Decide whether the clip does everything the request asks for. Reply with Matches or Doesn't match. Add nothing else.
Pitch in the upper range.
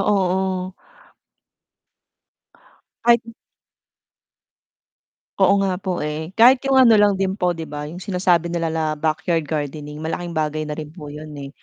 Doesn't match